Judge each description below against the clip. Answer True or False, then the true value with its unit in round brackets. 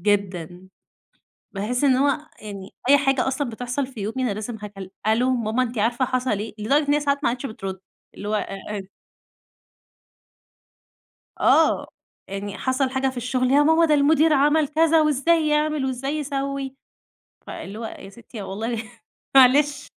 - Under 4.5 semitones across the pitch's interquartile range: False (5.0 semitones)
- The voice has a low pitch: False (255 Hz)